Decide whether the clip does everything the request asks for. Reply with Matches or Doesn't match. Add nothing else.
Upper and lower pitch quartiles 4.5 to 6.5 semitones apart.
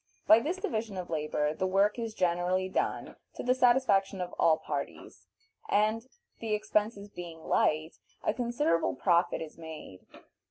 Matches